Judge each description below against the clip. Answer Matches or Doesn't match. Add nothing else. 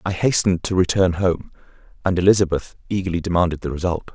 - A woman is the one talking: Doesn't match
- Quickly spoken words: Doesn't match